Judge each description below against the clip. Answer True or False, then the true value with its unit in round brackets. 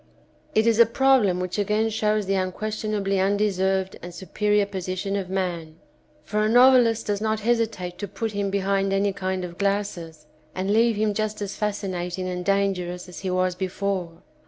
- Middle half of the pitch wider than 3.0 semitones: False (2.5 semitones)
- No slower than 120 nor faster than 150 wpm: False (170 wpm)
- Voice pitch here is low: False (195 Hz)